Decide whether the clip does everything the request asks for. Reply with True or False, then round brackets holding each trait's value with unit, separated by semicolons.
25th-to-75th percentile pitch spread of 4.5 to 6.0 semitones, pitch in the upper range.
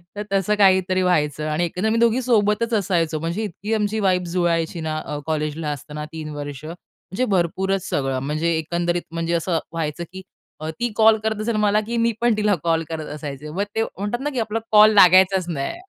False (4.9 semitones; 180 Hz)